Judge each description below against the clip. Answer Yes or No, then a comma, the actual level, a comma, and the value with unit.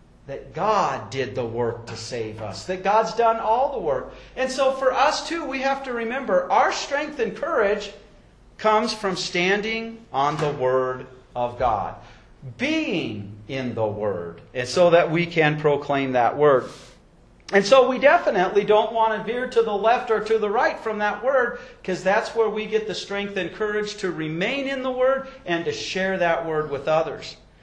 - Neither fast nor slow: Yes, average, 185 wpm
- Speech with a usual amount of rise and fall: No, wide, 7.1 semitones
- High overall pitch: Yes, high, 205 Hz